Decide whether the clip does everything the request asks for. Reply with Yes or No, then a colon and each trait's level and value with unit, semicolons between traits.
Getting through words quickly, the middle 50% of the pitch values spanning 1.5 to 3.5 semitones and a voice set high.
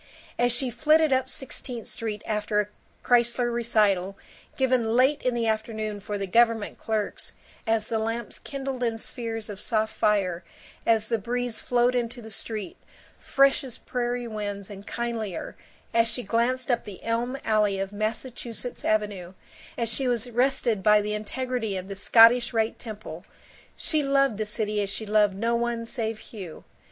No: average, 165 wpm; narrow, 2.5 semitones; high, 225 Hz